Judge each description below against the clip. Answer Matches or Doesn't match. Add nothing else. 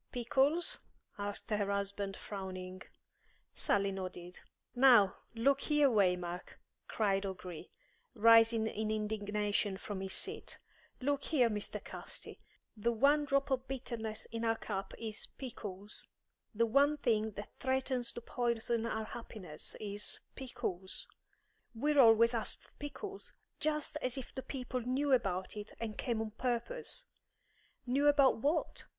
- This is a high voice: Matches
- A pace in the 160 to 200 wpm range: Doesn't match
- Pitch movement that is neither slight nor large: Matches